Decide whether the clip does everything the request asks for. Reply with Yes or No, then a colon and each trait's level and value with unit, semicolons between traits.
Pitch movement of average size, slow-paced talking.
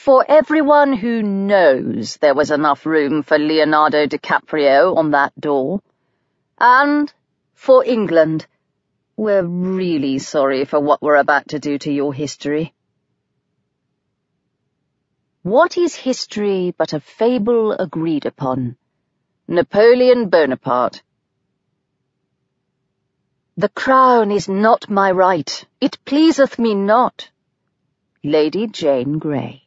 No: wide, 7.7 semitones; slow, 105 wpm